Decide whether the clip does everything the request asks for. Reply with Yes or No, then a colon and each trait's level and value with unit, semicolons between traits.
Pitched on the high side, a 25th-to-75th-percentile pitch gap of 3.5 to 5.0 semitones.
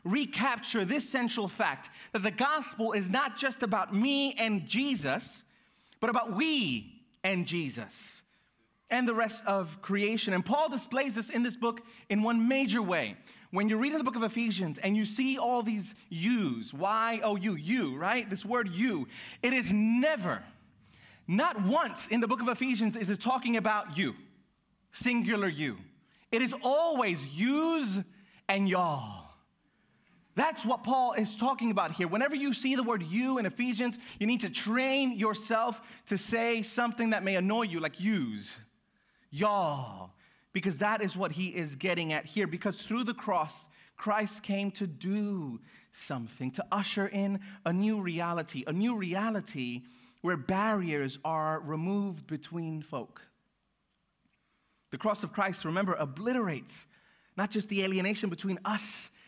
Yes: high, 215 Hz; average, 4.2 semitones